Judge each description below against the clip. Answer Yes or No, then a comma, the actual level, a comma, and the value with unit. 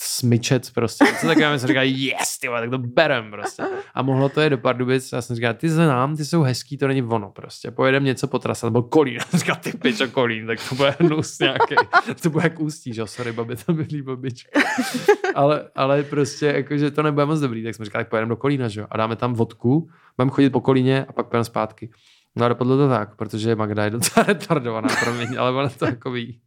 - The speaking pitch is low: Yes, low, 130 Hz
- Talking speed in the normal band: No, fast, 225 wpm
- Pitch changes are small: No, average, 4.2 semitones